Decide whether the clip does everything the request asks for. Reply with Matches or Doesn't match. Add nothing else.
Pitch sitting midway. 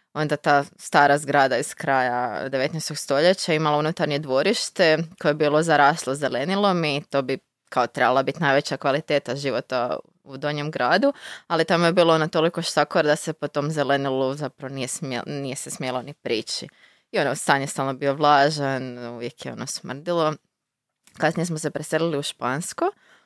Matches